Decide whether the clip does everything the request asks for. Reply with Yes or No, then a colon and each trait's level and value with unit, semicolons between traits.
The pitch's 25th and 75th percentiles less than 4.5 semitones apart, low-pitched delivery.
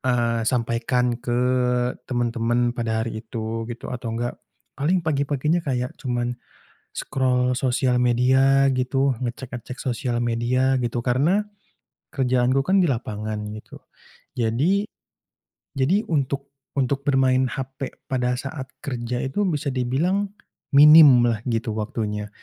Yes: narrow, 2.5 semitones; low, 125 Hz